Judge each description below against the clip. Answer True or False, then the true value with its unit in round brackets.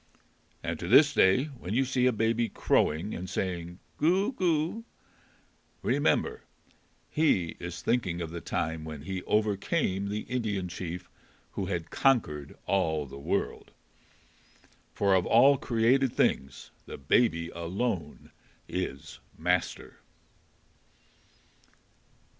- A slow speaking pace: True (115 wpm)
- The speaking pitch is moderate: False (95 Hz)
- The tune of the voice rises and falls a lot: True (6.7 semitones)